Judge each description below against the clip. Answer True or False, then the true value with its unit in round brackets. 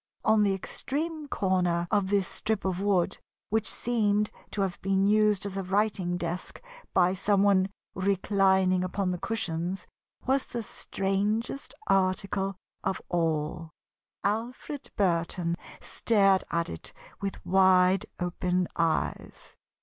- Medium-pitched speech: False (195 Hz)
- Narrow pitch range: True (2.3 semitones)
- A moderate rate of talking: False (125 wpm)